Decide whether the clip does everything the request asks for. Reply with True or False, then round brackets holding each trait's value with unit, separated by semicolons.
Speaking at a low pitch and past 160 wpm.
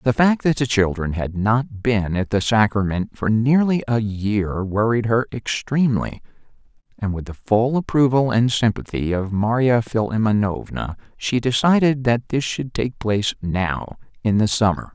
False (115 Hz; 155 wpm)